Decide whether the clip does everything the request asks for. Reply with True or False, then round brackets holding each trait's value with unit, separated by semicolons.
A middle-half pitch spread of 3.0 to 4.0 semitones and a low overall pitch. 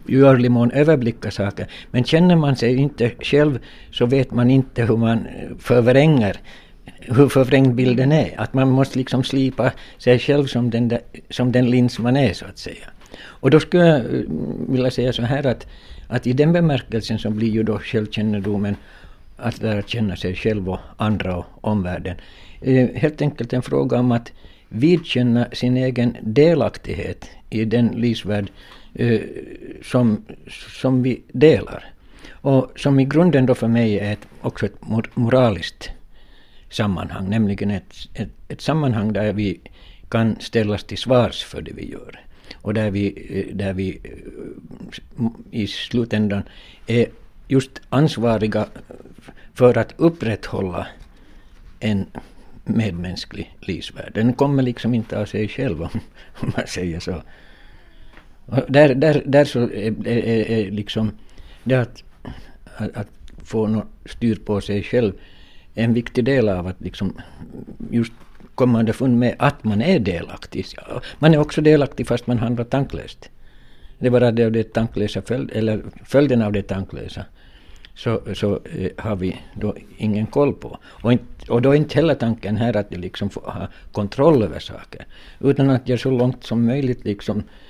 True (3.7 semitones; 115 Hz)